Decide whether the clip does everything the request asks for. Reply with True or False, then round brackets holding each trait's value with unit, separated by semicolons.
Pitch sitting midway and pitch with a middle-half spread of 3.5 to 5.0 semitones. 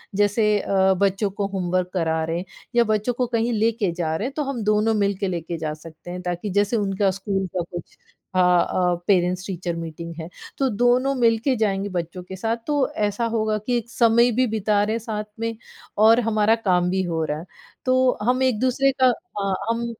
False (205 Hz; 4.3 semitones)